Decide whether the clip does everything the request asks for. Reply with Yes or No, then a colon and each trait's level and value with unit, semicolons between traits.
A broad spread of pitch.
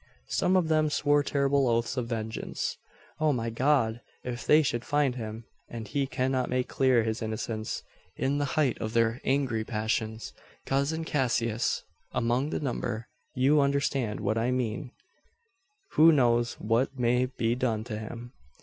No: average, 3.4 semitones